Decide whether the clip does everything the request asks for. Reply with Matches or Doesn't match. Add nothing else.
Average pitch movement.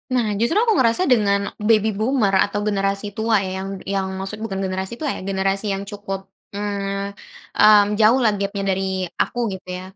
Doesn't match